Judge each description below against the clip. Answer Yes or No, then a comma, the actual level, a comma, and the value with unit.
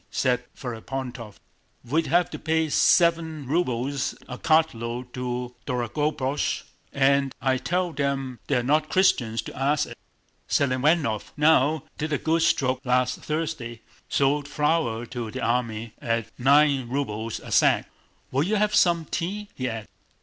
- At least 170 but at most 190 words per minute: No, slow, 135 wpm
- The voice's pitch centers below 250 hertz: Yes, low, 135 Hz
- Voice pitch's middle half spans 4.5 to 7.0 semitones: No, average, 4.1 semitones